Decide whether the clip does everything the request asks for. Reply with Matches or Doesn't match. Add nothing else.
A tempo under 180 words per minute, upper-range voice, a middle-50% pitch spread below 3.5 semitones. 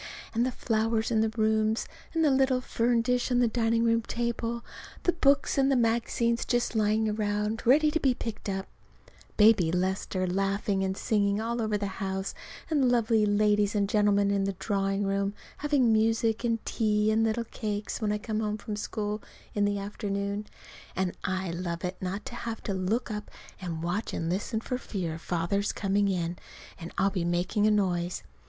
Doesn't match